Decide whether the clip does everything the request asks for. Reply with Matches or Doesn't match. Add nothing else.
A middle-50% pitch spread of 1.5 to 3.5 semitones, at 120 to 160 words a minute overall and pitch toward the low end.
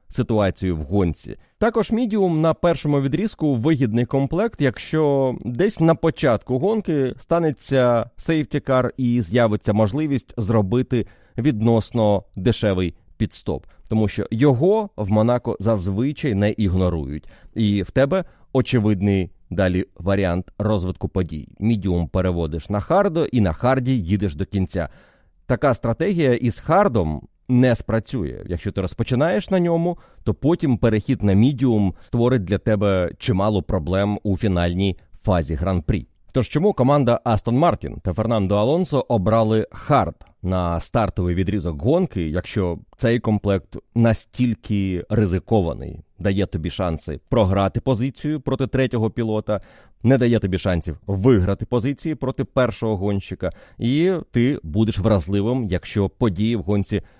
Doesn't match